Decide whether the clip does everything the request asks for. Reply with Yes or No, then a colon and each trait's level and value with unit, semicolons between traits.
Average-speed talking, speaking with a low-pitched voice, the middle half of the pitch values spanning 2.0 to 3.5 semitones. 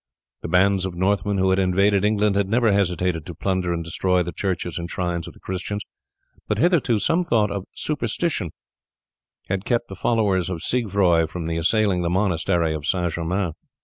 Yes: average, 180 wpm; very low, 95 Hz; average, 2.9 semitones